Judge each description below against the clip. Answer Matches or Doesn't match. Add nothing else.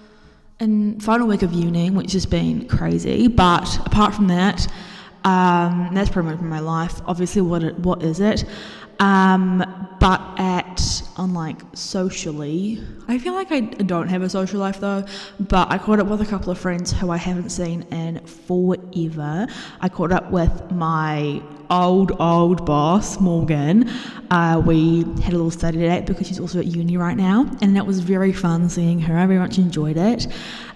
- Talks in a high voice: Doesn't match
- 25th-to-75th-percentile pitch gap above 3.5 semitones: Doesn't match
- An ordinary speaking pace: Matches